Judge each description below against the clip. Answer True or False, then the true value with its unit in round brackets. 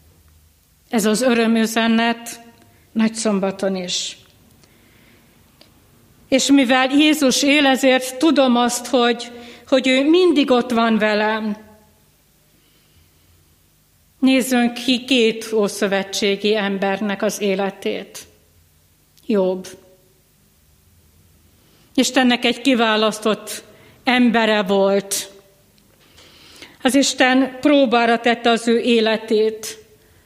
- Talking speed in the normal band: False (80 wpm)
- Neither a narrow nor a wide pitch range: True (4.1 semitones)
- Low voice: False (225 Hz)